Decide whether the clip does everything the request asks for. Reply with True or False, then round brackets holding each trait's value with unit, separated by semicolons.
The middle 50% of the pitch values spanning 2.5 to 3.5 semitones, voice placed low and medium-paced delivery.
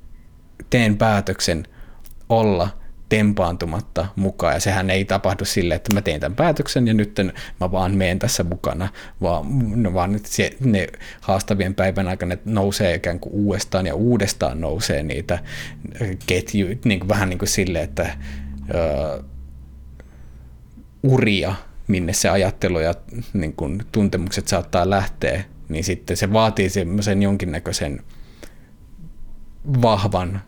True (3.1 semitones; 95 Hz; 120 wpm)